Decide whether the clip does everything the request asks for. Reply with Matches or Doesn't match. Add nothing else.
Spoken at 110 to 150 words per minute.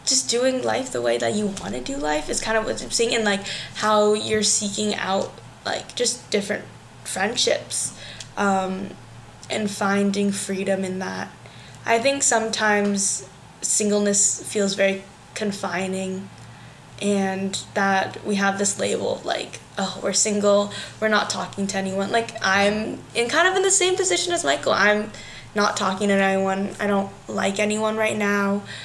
Doesn't match